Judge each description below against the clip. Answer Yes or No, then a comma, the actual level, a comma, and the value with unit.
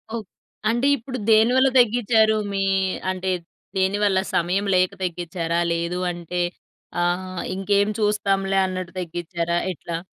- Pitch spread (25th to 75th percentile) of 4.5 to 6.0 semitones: No, average, 3.2 semitones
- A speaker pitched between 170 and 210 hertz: Yes, high, 190 Hz